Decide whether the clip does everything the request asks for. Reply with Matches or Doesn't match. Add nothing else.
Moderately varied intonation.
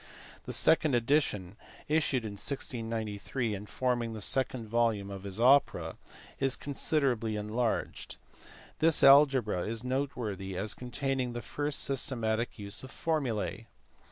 Matches